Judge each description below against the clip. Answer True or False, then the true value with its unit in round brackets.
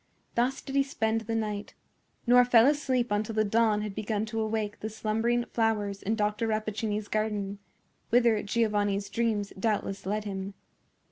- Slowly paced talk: False (155 wpm)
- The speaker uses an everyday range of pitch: False (1.8 semitones)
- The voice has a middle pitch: False (215 Hz)